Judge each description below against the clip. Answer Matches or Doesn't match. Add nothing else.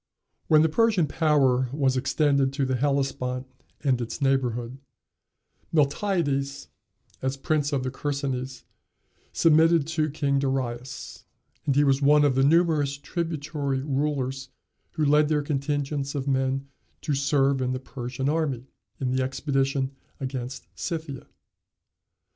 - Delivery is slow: Matches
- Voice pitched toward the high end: Doesn't match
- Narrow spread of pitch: Matches